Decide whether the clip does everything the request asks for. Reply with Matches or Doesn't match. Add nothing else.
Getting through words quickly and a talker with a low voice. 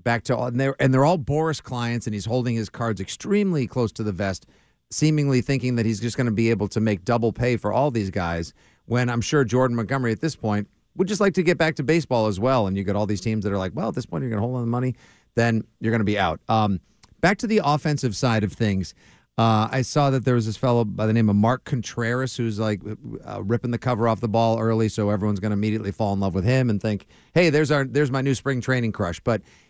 Matches